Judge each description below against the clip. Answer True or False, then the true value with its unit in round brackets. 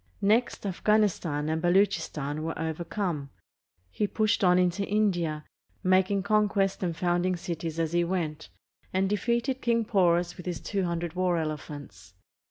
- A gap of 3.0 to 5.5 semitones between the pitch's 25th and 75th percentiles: True (3.6 semitones)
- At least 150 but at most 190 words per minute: False (140 wpm)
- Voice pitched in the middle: True (180 Hz)